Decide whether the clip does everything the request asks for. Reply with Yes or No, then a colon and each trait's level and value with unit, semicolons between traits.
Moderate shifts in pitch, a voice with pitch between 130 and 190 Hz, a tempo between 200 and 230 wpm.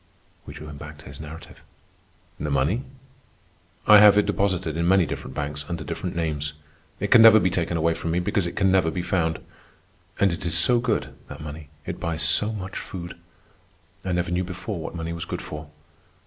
No: average, 3.3 semitones; very low, 85 Hz; fast, 205 wpm